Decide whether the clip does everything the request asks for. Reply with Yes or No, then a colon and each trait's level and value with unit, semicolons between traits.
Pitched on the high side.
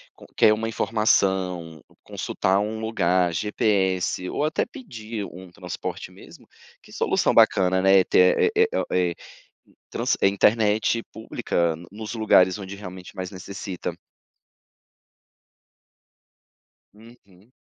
No: low, 100 Hz